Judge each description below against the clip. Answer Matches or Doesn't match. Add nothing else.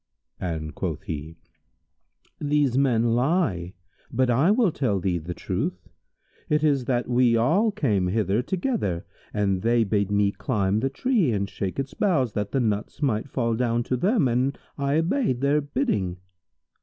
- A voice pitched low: Matches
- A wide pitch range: Matches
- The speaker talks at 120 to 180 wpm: Matches